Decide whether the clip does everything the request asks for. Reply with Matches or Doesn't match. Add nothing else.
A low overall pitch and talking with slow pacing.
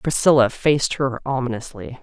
Matches